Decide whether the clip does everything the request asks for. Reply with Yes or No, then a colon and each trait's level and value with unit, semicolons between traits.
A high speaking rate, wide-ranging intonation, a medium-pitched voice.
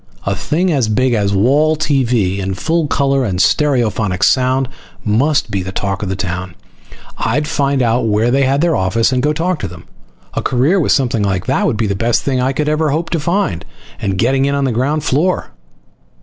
No: fast, 210 wpm; wide, 6.3 semitones; low, 130 Hz